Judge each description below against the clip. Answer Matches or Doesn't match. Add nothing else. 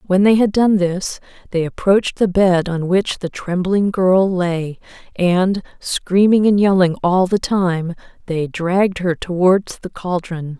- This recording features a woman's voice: Matches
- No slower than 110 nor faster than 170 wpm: Matches